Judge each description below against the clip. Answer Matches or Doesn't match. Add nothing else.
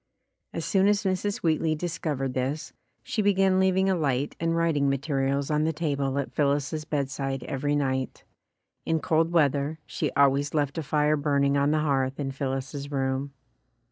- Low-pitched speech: Doesn't match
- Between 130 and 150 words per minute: Doesn't match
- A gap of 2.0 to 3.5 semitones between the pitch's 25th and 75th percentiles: Matches